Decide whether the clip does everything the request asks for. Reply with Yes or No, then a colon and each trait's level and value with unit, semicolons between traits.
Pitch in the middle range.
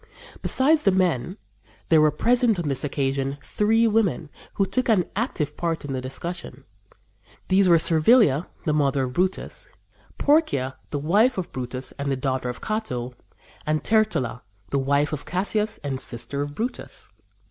Yes: medium, 155 Hz